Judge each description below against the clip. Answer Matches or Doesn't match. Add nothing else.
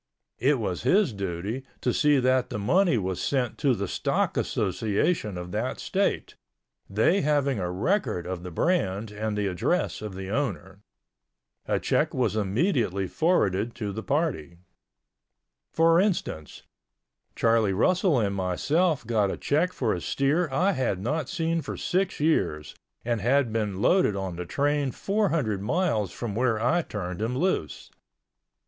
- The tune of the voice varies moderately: Doesn't match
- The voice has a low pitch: Matches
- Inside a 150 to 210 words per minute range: Matches